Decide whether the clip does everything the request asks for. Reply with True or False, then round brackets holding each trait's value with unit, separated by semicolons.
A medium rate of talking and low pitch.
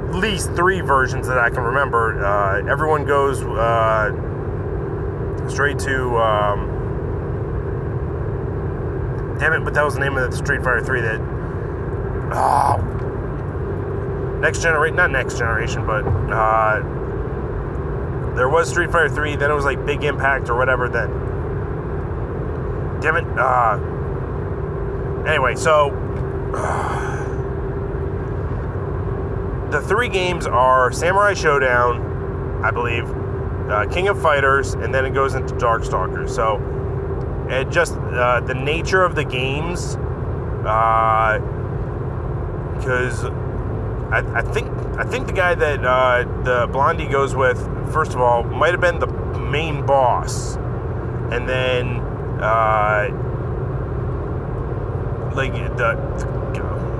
False (120 wpm; 125 Hz)